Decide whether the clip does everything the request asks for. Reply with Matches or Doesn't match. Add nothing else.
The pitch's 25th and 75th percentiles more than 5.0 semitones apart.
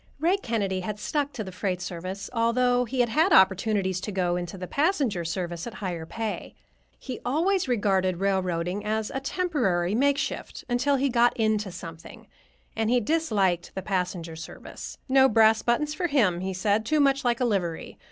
Matches